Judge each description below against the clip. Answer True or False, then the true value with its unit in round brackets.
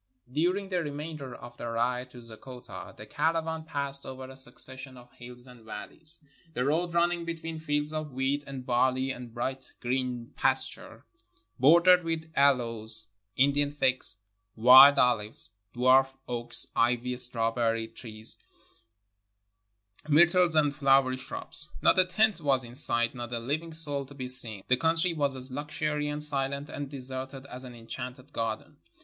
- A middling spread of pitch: True (3.3 semitones)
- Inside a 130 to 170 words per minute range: True (150 wpm)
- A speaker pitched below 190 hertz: True (135 Hz)